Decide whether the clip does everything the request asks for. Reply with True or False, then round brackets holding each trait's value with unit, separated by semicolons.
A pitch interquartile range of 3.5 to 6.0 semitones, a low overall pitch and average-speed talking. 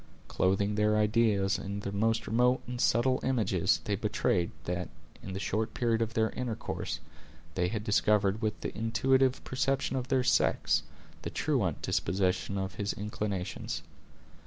False (3.0 semitones; 105 Hz; 150 wpm)